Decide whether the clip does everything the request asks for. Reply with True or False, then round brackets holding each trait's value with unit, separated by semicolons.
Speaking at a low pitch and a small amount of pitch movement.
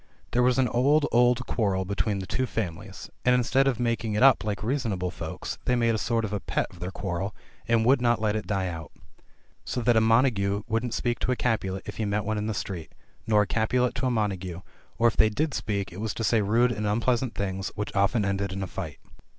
False (110 Hz; 3.5 semitones)